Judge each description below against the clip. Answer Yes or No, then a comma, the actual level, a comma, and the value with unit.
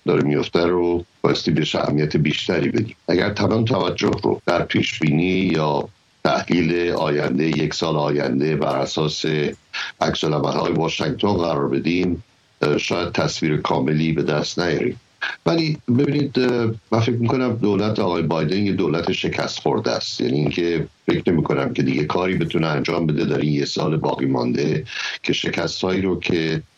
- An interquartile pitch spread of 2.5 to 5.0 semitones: No, wide, 5.5 semitones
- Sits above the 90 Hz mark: No, very low, 85 Hz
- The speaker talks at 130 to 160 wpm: Yes, average, 150 wpm